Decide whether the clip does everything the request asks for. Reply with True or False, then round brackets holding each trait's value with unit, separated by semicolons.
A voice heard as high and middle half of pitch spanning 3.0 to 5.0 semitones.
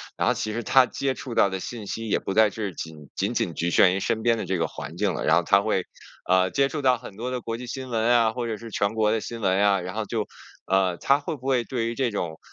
False (110 Hz; 4.1 semitones)